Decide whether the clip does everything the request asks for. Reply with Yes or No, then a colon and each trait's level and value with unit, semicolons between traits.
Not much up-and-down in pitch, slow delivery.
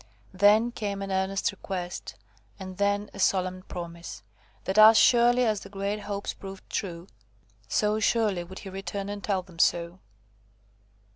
No: narrow, 2.0 semitones; average, 150 wpm